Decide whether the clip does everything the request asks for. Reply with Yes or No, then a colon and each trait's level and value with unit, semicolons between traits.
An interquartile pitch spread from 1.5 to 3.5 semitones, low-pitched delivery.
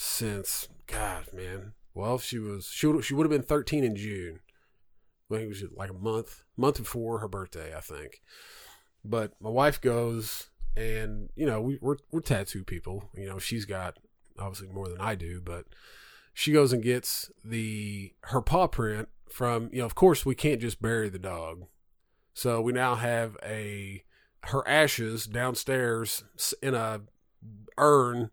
No: average, 4.4 semitones; low, 110 Hz